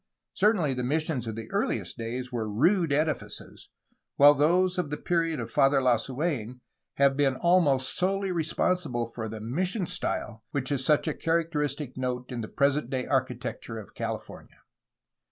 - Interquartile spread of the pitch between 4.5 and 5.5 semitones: Yes, average, 4.9 semitones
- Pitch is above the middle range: No, medium, 140 Hz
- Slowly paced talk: No, average, 155 wpm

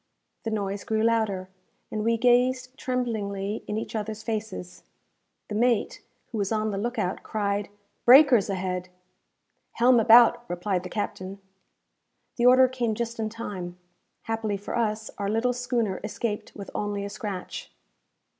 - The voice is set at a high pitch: Yes, high, 220 Hz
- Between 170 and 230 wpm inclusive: No, average, 145 wpm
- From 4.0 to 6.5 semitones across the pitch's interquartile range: No, average, 2.9 semitones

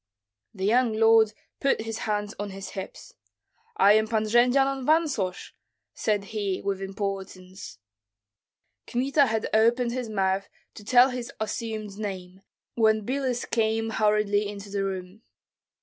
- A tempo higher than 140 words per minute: No, slow, 135 wpm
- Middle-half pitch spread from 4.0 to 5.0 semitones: No, average, 3.0 semitones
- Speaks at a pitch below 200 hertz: No, high, 215 Hz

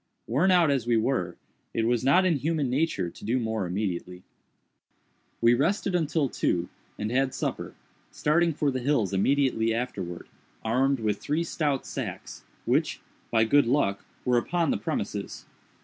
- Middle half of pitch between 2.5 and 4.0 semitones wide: No, average, 5.0 semitones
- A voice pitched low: Yes, low, 130 Hz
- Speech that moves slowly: No, average, 155 wpm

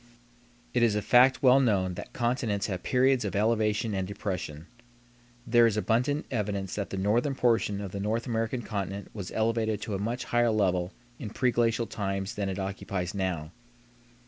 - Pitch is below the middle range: Yes, low, 105 Hz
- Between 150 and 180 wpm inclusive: Yes, average, 170 wpm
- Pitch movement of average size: Yes, average, 3.3 semitones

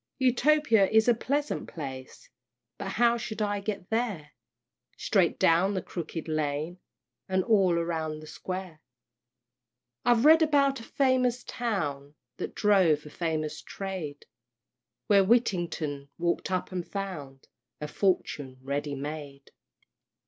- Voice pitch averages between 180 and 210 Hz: Yes, medium, 185 Hz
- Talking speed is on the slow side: Yes, slow, 125 wpm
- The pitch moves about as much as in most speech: No, wide, 6.5 semitones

